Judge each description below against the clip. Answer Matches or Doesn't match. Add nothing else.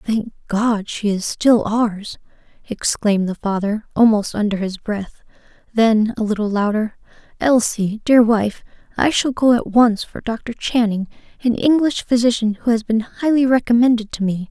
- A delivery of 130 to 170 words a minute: Matches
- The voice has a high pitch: Matches